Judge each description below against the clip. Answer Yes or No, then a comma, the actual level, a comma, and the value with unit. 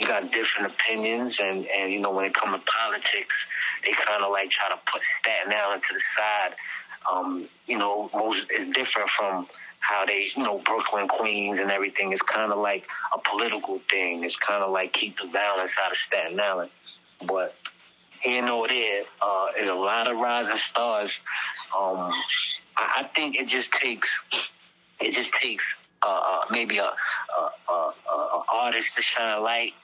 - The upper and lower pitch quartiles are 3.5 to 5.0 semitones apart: No, average, 3.1 semitones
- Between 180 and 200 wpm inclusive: Yes, average, 185 wpm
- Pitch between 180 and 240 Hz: No, low, 100 Hz